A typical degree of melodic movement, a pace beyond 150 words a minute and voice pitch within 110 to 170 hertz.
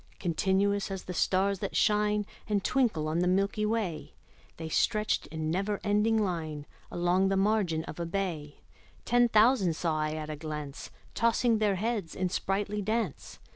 No: average, 4.4 semitones; average, 165 wpm; high, 195 Hz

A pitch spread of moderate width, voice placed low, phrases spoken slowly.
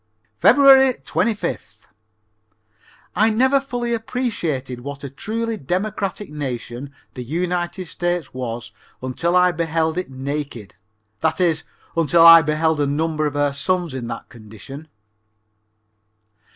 No: average, 4.7 semitones; medium, 160 Hz; slow, 120 wpm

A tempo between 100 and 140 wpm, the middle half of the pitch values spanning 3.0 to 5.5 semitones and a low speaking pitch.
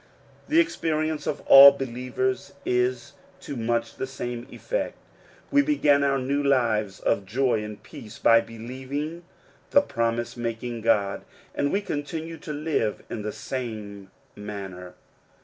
Yes: slow, 135 wpm; average, 4.1 semitones; low, 125 Hz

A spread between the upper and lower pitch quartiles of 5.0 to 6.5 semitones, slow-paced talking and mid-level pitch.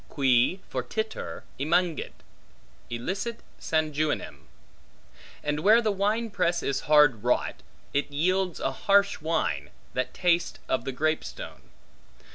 Yes: wide, 5.5 semitones; slow, 115 wpm; medium, 160 Hz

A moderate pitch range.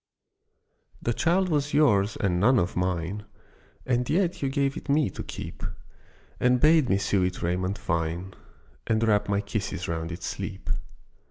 No: wide, 6.9 semitones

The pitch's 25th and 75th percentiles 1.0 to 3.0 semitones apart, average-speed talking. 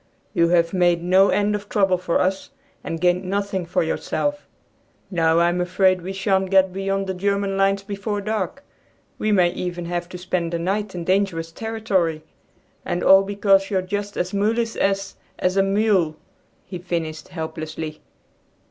Yes: narrow, 2.4 semitones; average, 165 wpm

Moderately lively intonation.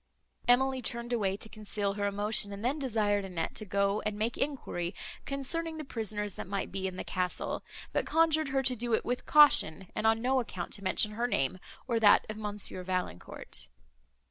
Yes: average, 3.9 semitones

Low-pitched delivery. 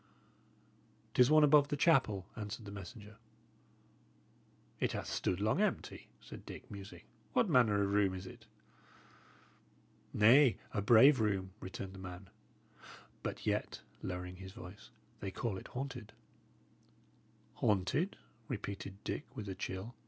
Yes: low, 105 Hz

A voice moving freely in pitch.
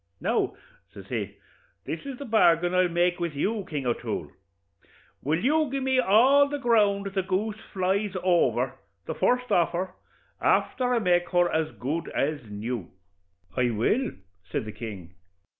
Yes: wide, 6.5 semitones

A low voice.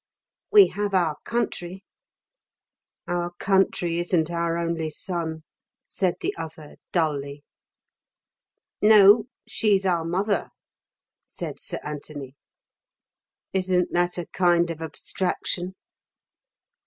No: medium, 175 Hz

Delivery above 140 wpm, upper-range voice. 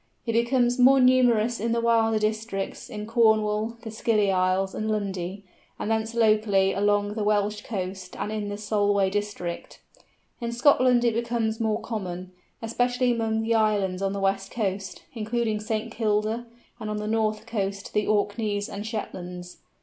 Yes: average, 165 wpm; high, 215 Hz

